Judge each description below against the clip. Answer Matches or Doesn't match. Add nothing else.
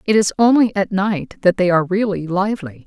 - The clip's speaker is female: Matches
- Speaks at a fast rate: Matches